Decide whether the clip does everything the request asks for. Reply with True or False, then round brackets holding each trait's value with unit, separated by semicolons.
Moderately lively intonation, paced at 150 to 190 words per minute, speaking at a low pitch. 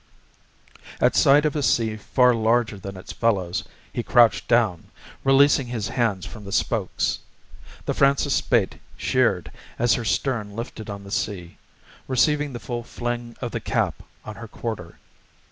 True (3.4 semitones; 155 wpm; 115 Hz)